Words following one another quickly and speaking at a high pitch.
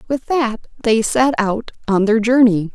No: average, 175 wpm; high, 230 Hz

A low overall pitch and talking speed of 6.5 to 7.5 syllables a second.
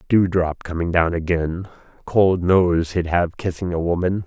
No: very low, 85 Hz; 4.3 syllables/s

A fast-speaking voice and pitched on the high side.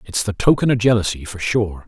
No: fast, 225 wpm; low, 105 Hz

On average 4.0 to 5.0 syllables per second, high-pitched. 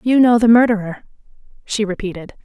No: 5.8 syllables/s; high, 215 Hz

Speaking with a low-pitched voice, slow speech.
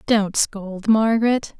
No: high, 215 Hz; slow, 115 wpm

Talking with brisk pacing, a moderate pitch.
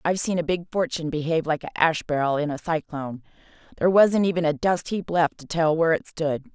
Yes: fast, 220 wpm; medium, 160 Hz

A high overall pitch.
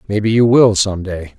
No: low, 105 Hz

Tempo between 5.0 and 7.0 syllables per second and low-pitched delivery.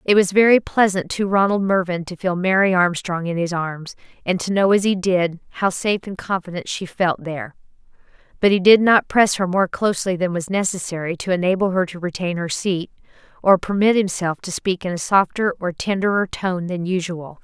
No: 5.3 syllables/s; medium, 185 Hz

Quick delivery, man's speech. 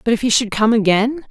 No: fast, 275 wpm; female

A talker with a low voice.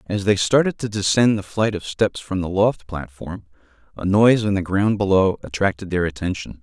Yes: low, 100 Hz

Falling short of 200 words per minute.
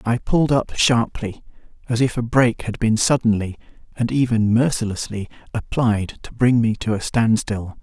Yes: average, 155 wpm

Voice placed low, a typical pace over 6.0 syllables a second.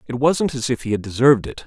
Yes: low, 125 Hz; 6.5 syllables/s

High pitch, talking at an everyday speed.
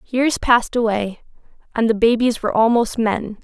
Yes: high, 230 Hz; average, 155 wpm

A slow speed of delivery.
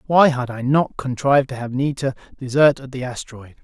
No: average, 200 wpm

